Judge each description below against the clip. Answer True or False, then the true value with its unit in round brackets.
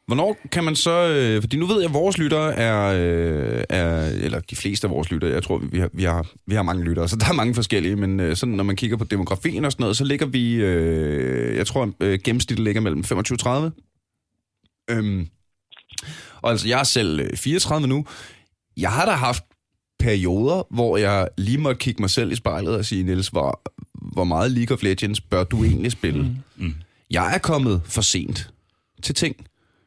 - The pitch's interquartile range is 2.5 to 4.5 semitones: False (5.4 semitones)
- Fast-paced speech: False (195 wpm)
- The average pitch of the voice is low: True (110 Hz)